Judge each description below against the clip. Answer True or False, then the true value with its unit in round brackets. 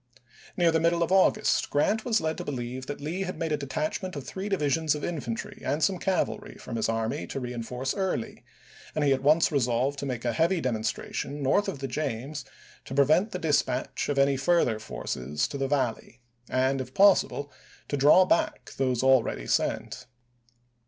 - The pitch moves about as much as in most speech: True (4.6 semitones)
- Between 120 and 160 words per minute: False (185 wpm)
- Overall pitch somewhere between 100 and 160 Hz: True (140 Hz)